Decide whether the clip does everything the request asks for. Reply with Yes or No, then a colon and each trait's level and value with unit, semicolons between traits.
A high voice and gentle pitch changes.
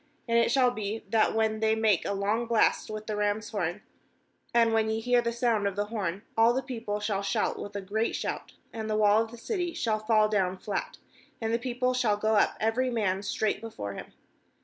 Yes: high, 220 Hz; narrow, 2.0 semitones